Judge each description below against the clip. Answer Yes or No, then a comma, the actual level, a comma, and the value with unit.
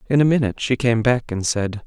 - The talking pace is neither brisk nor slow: No, fast, 255 wpm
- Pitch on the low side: Yes, low, 120 Hz